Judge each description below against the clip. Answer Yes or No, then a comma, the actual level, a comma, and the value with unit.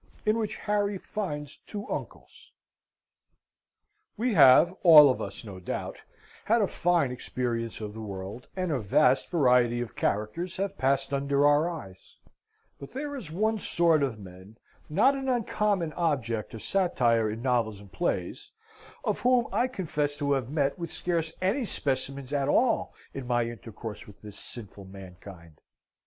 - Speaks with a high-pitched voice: No, medium, 140 Hz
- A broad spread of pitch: Yes, wide, 8.2 semitones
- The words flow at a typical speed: Yes, average, 155 wpm